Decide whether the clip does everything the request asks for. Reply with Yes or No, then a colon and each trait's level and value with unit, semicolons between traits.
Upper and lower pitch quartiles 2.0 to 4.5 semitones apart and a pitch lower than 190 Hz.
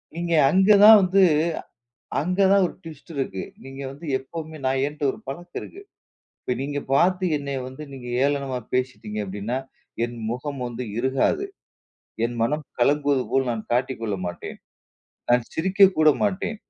No: average, 5.1 semitones; medium, 140 Hz